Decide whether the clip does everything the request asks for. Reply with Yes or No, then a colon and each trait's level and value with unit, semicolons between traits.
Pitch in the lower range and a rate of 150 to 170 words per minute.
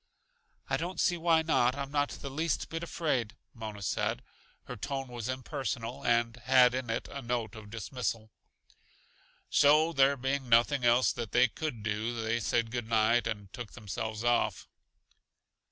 Yes: low, 120 Hz; average, 160 wpm